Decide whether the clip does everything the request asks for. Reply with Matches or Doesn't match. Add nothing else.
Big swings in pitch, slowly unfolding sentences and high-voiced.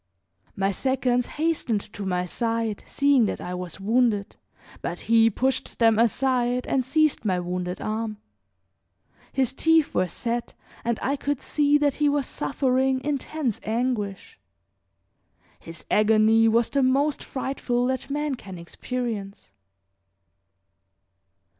Doesn't match